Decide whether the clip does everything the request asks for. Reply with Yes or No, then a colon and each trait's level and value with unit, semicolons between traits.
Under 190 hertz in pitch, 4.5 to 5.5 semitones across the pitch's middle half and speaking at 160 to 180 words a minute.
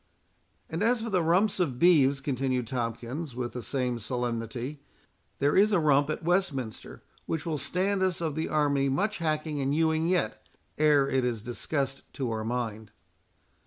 Yes: medium, 140 Hz; average, 4.9 semitones; average, 165 wpm